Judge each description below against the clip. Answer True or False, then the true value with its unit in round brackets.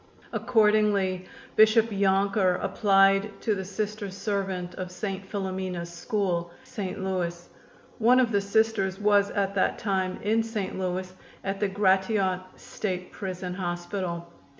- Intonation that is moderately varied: False (2.1 semitones)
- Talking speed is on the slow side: True (125 wpm)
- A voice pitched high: True (195 Hz)